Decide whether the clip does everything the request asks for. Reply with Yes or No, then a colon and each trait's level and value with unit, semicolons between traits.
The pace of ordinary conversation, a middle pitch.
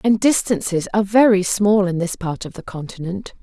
No: average, 195 wpm; high, 195 Hz